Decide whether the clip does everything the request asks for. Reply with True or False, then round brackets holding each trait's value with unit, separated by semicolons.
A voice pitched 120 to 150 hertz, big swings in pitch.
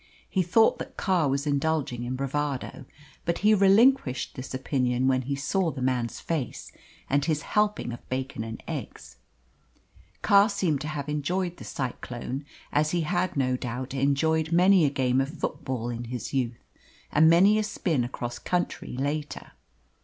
False (140 Hz; 4.9 semitones)